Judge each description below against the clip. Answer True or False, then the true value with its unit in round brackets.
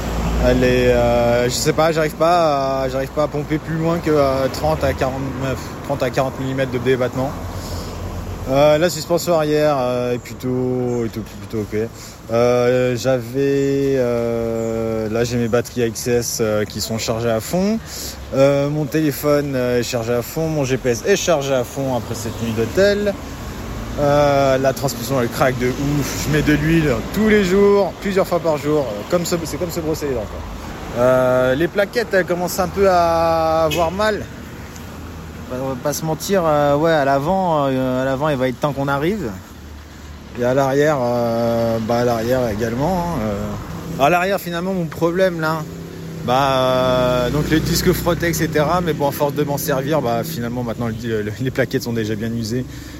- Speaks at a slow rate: False (185 wpm)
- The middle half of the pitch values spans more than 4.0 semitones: True (4.8 semitones)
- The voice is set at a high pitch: False (135 Hz)